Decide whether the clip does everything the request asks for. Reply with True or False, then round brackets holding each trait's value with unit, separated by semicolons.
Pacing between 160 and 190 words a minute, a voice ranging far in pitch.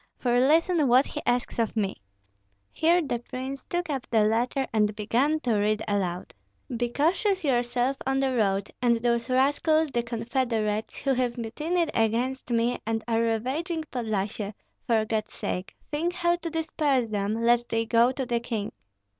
False (165 wpm; 3.6 semitones)